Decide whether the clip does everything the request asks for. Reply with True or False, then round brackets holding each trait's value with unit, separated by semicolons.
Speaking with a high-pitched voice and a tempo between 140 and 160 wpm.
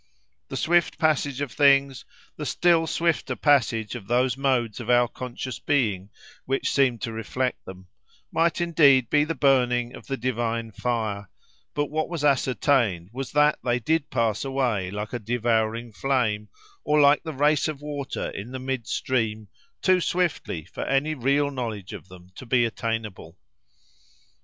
False (125 Hz; 155 wpm)